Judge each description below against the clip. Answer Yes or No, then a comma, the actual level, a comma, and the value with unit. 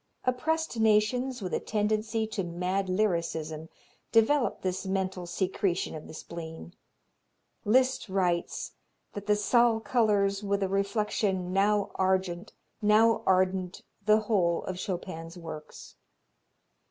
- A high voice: Yes, high, 195 Hz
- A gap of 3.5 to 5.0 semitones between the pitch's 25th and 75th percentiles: No, average, 3.1 semitones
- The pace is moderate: No, slow, 115 wpm